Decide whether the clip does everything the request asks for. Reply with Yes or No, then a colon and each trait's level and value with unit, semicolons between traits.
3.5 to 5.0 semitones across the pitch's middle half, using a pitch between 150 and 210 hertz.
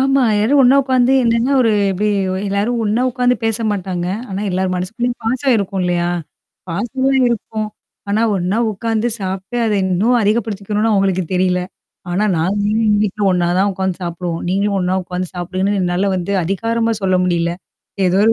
Yes: average, 3.8 semitones; high, 200 Hz